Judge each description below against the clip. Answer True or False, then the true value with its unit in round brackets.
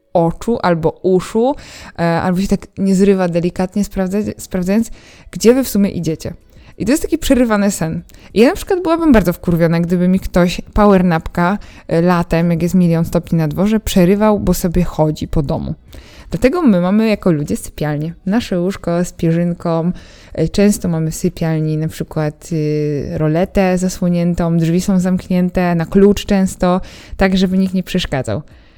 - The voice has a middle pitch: True (180 Hz)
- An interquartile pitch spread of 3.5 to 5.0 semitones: False (3.1 semitones)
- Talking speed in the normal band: False (165 wpm)